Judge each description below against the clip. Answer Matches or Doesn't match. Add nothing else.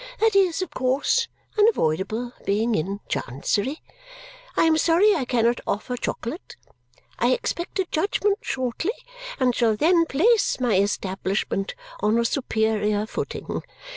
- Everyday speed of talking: Doesn't match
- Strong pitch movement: Matches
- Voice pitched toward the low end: Doesn't match